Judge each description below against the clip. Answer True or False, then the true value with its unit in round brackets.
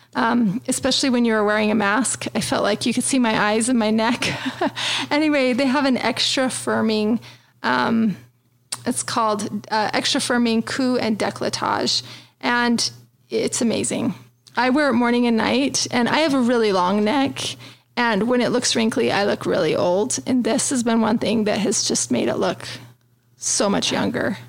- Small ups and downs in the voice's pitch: False (3.0 semitones)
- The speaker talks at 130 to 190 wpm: True (180 wpm)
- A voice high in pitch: True (230 Hz)